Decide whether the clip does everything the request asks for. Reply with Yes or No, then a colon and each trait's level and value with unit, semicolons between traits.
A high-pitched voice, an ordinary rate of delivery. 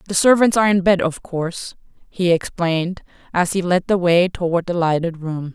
No: medium, 175 Hz; average, 195 wpm